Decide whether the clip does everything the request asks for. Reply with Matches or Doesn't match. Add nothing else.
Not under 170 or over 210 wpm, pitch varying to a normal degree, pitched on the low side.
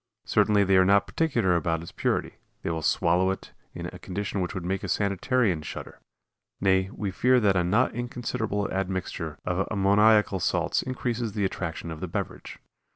Matches